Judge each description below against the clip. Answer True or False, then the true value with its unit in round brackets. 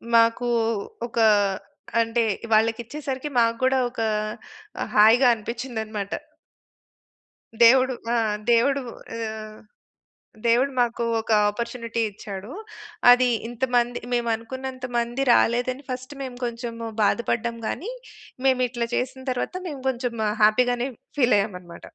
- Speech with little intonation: True (2.0 semitones)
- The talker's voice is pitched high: True (240 Hz)